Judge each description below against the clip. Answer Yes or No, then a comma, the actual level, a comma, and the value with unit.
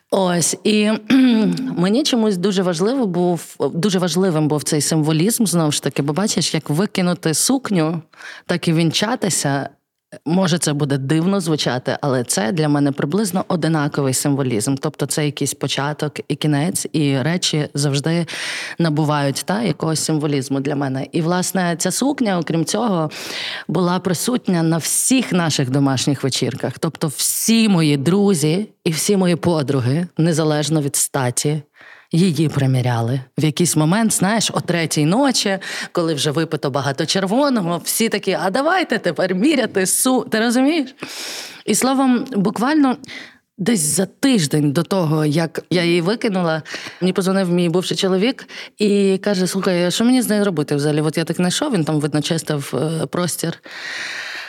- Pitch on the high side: No, medium, 170 Hz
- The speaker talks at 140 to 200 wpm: Yes, average, 145 wpm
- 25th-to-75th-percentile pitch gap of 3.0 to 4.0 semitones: No, average, 4.8 semitones